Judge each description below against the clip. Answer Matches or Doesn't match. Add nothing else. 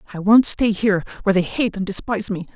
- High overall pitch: Matches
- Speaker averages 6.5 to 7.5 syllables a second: Matches